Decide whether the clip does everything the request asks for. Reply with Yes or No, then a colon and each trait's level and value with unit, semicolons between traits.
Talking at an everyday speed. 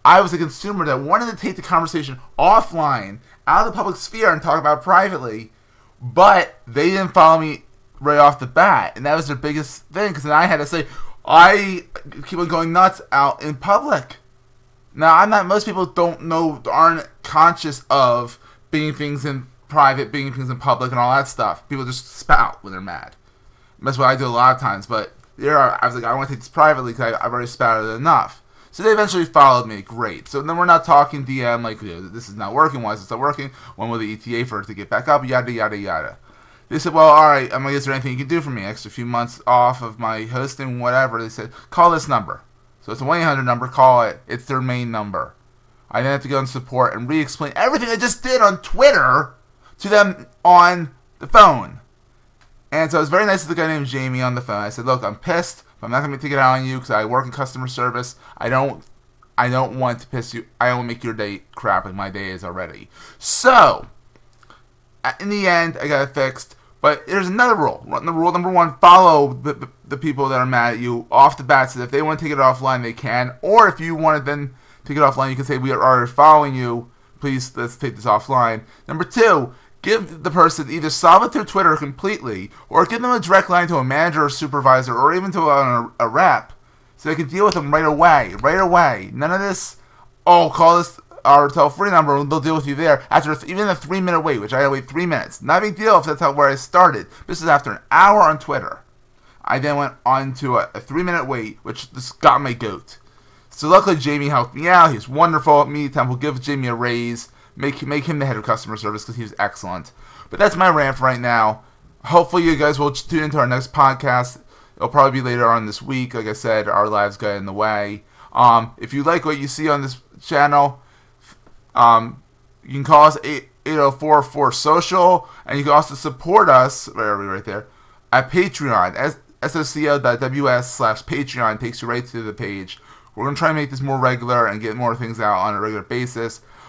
No: fast, 230 wpm